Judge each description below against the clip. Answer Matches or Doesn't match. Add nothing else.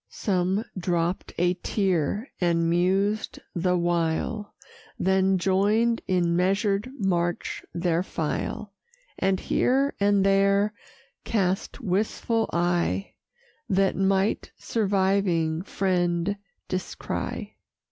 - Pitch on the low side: Doesn't match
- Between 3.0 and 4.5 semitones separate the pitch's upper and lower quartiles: Doesn't match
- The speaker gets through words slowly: Matches